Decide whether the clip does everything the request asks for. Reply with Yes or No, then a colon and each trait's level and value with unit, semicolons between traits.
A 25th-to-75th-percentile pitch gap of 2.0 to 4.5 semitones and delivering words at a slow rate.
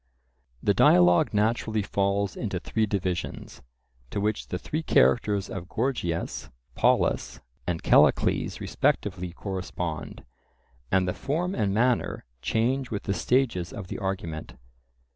Yes: average, 3.8 semitones; slow, 125 wpm